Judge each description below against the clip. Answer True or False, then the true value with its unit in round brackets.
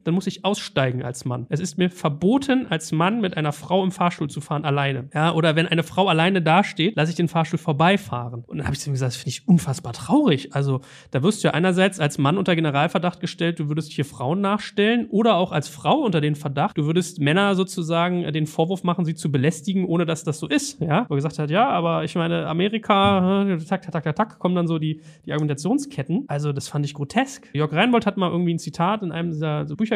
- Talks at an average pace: False (240 wpm)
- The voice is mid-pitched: True (165 Hz)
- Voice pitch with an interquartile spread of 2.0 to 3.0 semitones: False (4.0 semitones)